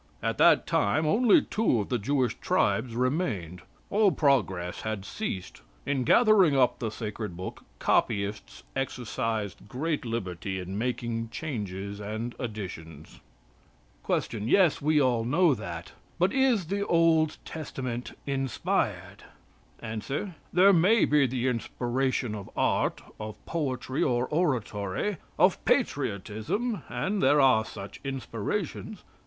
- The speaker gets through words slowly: Yes, slow, 120 wpm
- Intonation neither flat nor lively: No, wide, 6.7 semitones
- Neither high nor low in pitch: No, low, 125 Hz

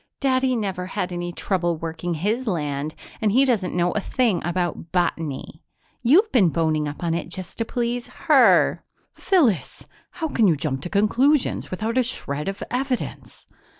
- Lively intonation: Yes, wide, 6.5 semitones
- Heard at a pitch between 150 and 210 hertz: Yes, medium, 185 Hz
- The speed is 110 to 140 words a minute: No, average, 165 wpm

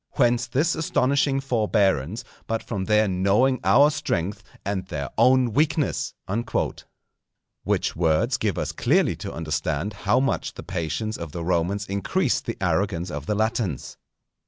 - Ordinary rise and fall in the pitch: No, wide, 6.1 semitones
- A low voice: Yes, low, 105 Hz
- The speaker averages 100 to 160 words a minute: Yes, average, 140 wpm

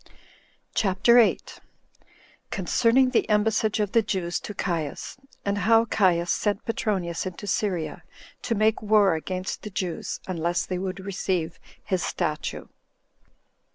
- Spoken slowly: Yes, slow, 130 wpm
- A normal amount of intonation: Yes, average, 3.5 semitones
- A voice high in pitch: Yes, high, 195 Hz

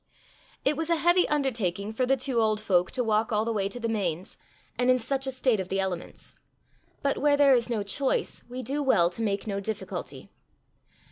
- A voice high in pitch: Yes, high, 230 Hz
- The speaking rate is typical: No, fast, 210 wpm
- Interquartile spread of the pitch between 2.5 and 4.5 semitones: No, average, 5.0 semitones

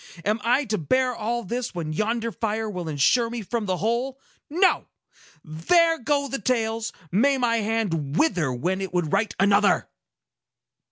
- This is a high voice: Yes, high, 225 Hz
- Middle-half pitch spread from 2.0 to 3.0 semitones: No, average, 4.8 semitones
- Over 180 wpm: No, average, 160 wpm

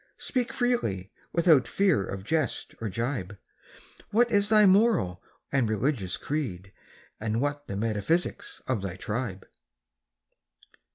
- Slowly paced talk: Yes, slow, 120 wpm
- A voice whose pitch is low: Yes, low, 130 Hz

